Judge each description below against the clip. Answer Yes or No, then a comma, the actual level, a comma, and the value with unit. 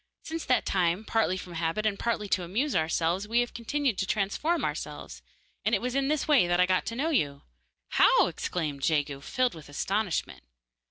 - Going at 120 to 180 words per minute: No, average, 195 wpm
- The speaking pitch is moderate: No, high, 200 Hz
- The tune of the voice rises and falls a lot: Yes, wide, 6.4 semitones